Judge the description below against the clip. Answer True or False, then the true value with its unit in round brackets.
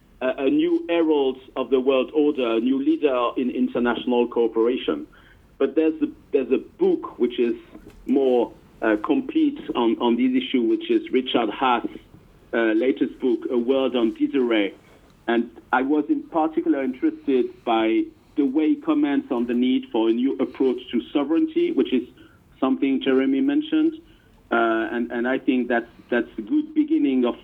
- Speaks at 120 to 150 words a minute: False (165 wpm)